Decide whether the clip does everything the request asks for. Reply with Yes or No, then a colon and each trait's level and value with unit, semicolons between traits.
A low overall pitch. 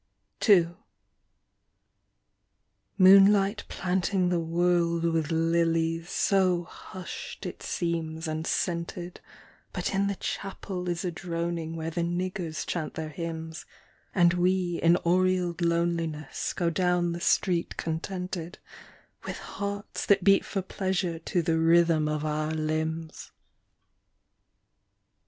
No: medium, 170 Hz